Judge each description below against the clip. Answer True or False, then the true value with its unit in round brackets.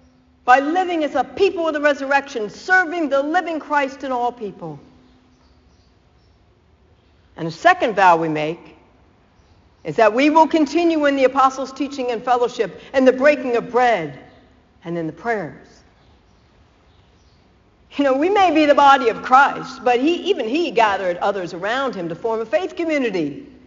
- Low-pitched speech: False (245 Hz)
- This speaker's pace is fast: False (160 wpm)